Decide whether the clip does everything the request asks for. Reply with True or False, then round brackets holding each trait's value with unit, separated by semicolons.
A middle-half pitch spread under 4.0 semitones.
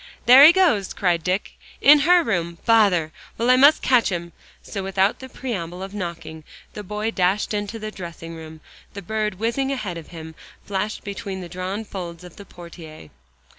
False (4.5 semitones)